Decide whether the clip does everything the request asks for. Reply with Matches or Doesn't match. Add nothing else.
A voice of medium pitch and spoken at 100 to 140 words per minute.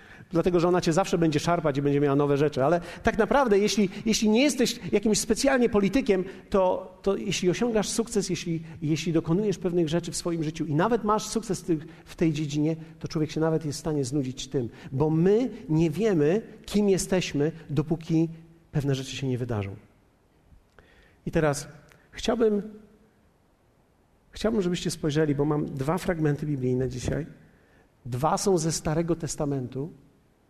Doesn't match